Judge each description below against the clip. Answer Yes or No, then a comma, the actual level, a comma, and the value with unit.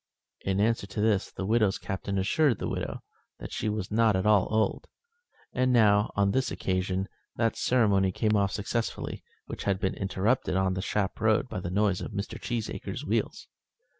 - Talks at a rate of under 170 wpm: No, average, 180 wpm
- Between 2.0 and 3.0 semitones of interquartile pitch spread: Yes, narrow, 2.4 semitones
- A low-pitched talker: Yes, low, 100 Hz